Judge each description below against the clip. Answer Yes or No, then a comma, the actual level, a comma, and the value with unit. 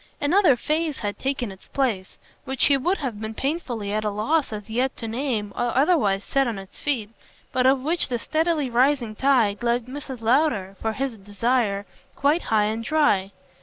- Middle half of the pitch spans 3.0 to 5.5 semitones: Yes, average, 4.8 semitones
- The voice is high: Yes, high, 245 Hz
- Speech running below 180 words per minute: No, average, 185 wpm